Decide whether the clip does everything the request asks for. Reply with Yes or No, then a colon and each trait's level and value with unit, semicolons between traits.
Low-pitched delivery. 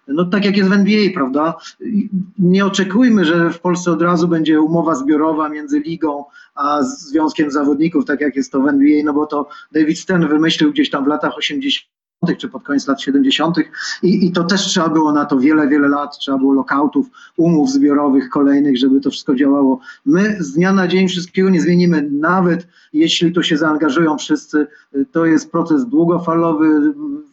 No: medium, 165 Hz